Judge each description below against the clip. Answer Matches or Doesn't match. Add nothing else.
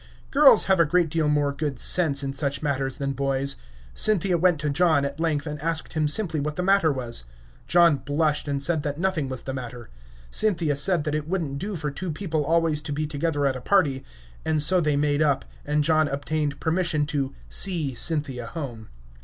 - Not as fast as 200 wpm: Doesn't match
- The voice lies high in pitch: Doesn't match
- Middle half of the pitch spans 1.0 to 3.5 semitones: Matches